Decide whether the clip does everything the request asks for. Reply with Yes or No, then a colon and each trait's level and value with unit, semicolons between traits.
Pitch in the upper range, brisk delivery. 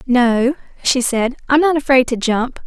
No: very high, 255 Hz; average, 180 wpm